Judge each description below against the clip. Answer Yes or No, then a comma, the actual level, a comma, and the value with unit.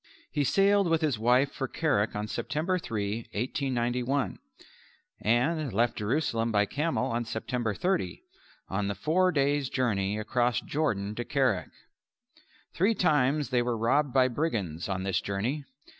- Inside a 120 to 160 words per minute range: Yes, average, 145 wpm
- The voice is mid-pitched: No, low, 125 Hz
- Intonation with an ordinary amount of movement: No, wide, 5.7 semitones